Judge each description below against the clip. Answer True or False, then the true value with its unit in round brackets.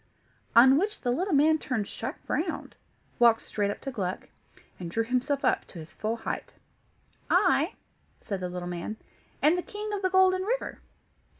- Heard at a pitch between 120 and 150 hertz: False (255 Hz)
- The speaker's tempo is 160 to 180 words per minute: True (175 wpm)